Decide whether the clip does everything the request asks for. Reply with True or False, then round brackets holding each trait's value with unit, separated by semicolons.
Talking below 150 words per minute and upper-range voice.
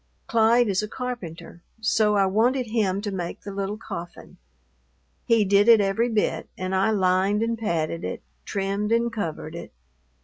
False (165 wpm; 205 Hz)